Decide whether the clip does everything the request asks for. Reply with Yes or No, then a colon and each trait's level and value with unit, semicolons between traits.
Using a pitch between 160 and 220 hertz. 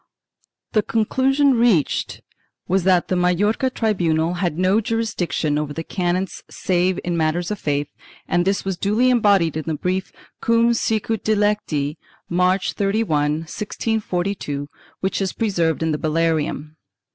Yes: medium, 185 Hz